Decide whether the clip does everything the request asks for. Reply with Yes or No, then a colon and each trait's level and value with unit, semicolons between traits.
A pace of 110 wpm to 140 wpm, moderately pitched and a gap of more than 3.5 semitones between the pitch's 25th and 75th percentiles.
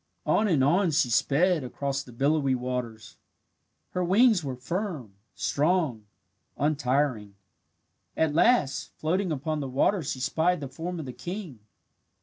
Yes: slow, 135 wpm; medium, 145 Hz; wide, 5.4 semitones